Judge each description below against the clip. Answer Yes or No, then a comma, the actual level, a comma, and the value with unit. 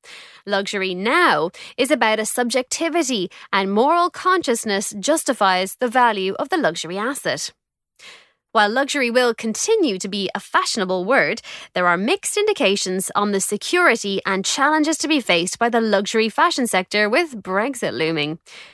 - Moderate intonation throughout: No, wide, 6.4 semitones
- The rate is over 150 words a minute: No, average, 145 wpm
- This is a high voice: Yes, high, 220 Hz